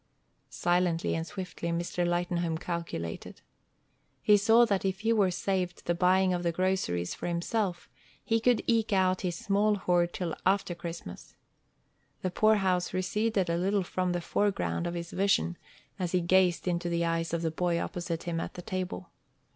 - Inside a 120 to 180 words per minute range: Yes, average, 170 wpm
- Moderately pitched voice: Yes, medium, 180 Hz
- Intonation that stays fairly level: Yes, narrow, 2.1 semitones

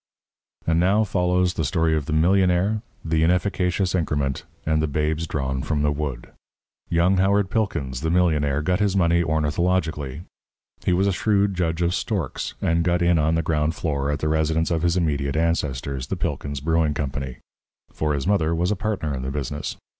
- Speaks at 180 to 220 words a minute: Yes, average, 185 wpm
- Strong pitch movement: No, average, 3.3 semitones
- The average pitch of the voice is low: Yes, very low, 80 Hz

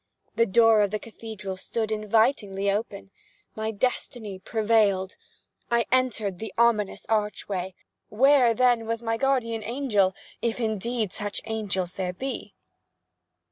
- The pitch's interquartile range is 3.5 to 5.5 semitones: No, narrow, 2.6 semitones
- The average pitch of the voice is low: No, high, 220 Hz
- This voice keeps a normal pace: No, slow, 120 wpm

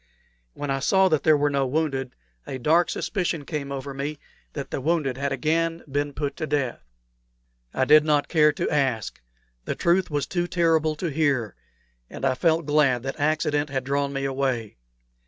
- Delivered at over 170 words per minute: Yes, average, 180 wpm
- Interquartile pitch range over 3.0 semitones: No, narrow, 2.5 semitones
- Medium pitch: Yes, medium, 145 Hz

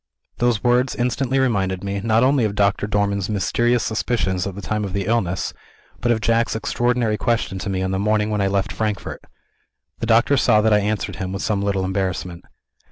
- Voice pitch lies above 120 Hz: No, low, 105 Hz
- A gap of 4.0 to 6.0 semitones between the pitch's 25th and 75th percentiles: No, average, 3.1 semitones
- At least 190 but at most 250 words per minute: Yes, average, 200 wpm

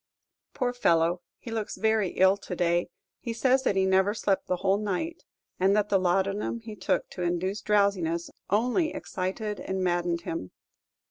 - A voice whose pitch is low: No, high, 195 Hz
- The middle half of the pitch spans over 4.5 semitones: No, average, 3.1 semitones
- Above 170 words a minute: No, average, 165 wpm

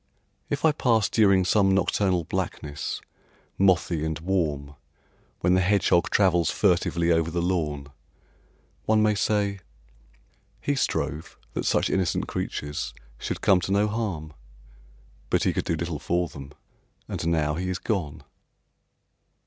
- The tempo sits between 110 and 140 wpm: Yes, slow, 135 wpm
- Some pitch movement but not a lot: Yes, average, 3.9 semitones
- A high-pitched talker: No, very low, 90 Hz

